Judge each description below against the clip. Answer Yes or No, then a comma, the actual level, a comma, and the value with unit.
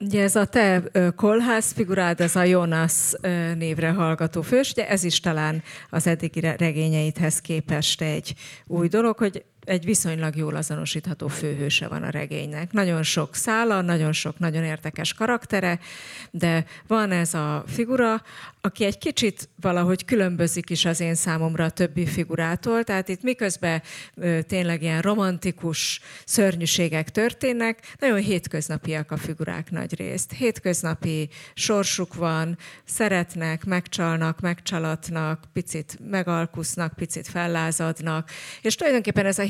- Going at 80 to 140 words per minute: Yes, average, 130 wpm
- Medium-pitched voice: Yes, medium, 170 Hz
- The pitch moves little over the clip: No, average, 3.5 semitones